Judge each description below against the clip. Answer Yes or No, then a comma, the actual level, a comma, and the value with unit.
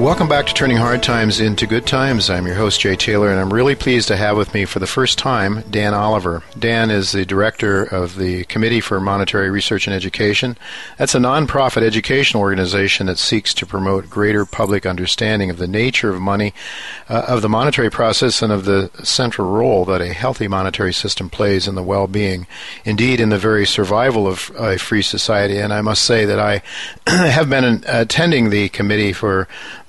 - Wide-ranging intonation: No, average, 2.9 semitones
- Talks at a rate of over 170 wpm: Yes, average, 195 wpm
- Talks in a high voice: No, low, 105 Hz